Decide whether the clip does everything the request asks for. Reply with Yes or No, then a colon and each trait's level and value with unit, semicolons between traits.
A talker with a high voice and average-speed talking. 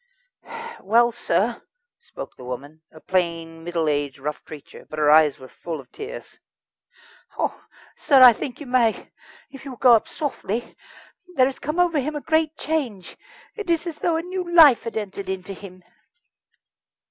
Yes: high, 230 Hz; average, 170 wpm